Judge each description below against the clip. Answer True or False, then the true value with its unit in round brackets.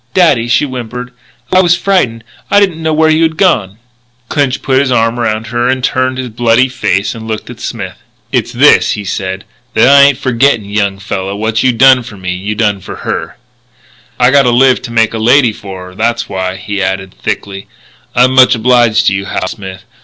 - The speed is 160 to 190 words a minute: False (205 wpm)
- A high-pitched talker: False (120 Hz)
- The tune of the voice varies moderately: True (4.2 semitones)